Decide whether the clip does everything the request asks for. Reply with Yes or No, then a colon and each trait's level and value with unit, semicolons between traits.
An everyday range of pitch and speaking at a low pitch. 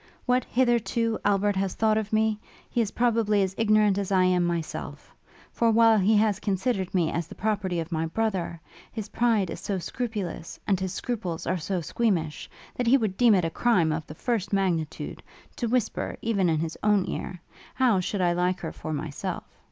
No: average, 4.0 semitones; high, 200 Hz